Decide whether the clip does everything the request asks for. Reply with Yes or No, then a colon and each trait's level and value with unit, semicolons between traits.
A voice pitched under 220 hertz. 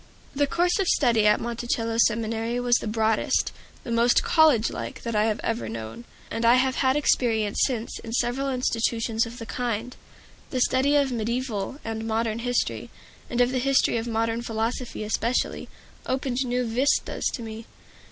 No: high, 235 Hz